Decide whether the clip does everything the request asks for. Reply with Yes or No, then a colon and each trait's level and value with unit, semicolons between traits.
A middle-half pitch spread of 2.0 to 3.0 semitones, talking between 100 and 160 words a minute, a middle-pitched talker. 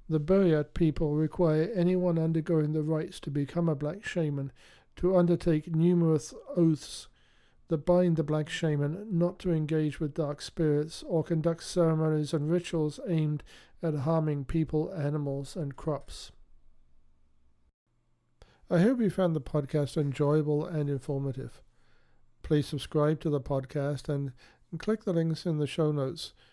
Yes: narrow, 2.6 semitones; average, 140 wpm; medium, 155 Hz